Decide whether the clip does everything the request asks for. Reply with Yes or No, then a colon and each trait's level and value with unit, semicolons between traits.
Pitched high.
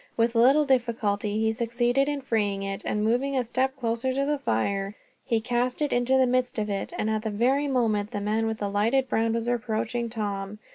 Yes: high, 230 Hz